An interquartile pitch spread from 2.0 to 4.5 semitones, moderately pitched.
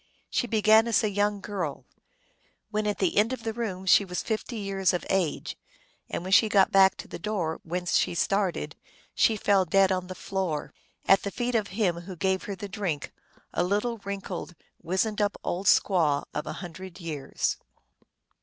No: average, 2.7 semitones; high, 195 Hz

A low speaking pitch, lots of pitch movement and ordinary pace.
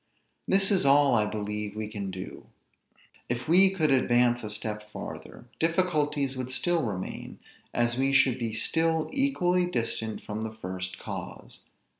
Yes: low, 125 Hz; wide, 7.2 semitones; average, 150 wpm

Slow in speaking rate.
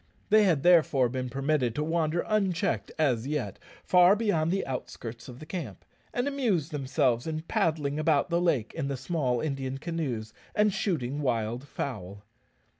No: average, 160 wpm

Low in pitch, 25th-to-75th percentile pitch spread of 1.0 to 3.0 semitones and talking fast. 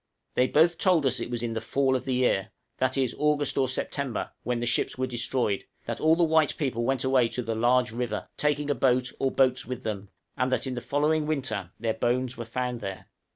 Yes: low, 130 Hz; narrow, 2.6 semitones; fast, 230 wpm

